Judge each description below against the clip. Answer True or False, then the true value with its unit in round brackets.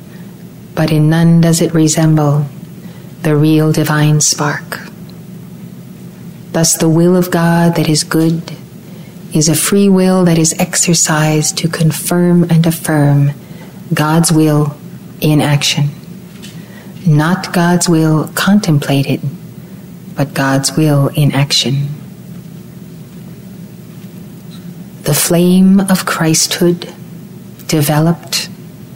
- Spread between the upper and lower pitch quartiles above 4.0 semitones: False (2.5 semitones)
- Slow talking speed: True (95 wpm)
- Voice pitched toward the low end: False (170 Hz)